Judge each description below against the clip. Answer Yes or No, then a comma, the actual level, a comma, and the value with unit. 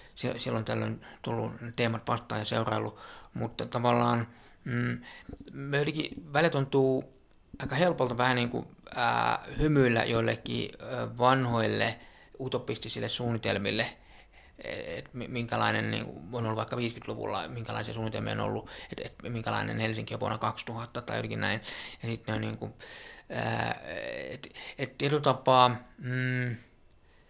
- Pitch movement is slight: Yes, narrow, 2.3 semitones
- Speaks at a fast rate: No, average, 125 wpm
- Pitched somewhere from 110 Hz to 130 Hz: Yes, low, 120 Hz